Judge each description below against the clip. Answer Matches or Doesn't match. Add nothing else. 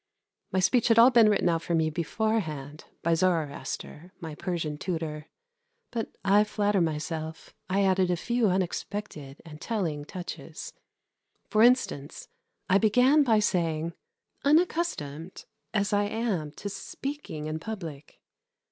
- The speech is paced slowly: Matches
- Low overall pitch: Doesn't match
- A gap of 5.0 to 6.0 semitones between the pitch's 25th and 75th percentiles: Matches